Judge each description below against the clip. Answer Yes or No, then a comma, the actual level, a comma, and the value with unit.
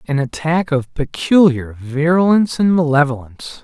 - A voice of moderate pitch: Yes, medium, 150 Hz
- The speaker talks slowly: Yes, slow, 115 wpm